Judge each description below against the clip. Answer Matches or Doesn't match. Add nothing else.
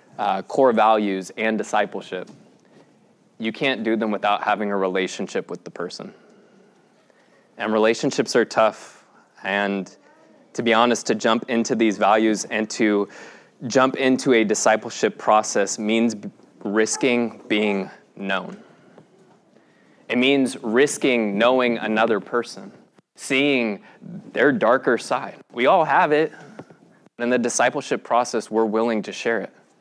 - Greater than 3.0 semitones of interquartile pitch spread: Doesn't match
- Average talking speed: Doesn't match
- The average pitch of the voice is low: Matches